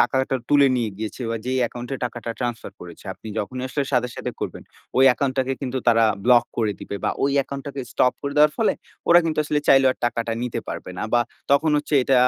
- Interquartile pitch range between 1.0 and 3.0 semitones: Yes, average, 2.7 semitones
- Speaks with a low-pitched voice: Yes, low, 130 Hz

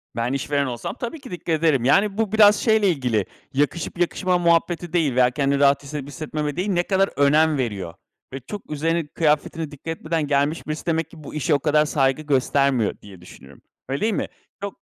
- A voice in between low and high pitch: Yes, medium, 150 Hz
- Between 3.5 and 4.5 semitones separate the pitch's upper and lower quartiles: Yes, average, 3.9 semitones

